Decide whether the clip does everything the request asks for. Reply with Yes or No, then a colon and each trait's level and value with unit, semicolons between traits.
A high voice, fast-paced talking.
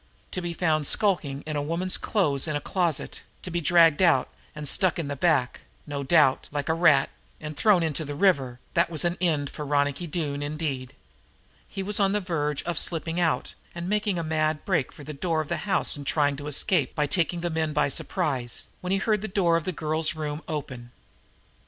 No: medium, 155 Hz; fast, 210 wpm